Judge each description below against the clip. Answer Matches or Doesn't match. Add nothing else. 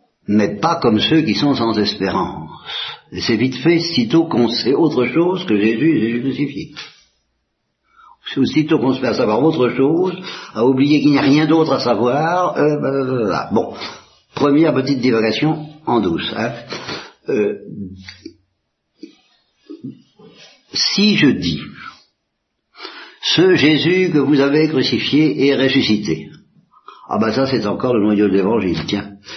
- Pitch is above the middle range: Doesn't match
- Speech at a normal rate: Matches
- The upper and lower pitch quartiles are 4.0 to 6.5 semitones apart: Matches